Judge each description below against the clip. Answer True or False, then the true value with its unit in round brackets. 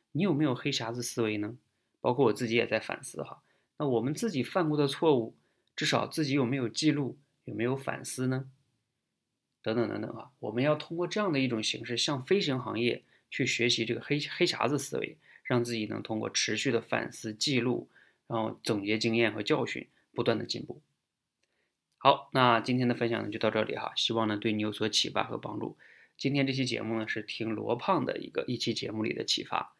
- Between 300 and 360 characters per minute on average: True (305 characters per minute)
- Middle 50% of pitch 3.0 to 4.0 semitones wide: True (3.7 semitones)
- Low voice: True (120 Hz)